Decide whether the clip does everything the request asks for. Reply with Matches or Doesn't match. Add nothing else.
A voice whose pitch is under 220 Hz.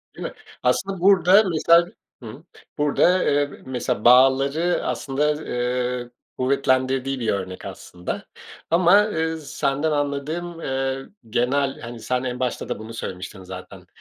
Matches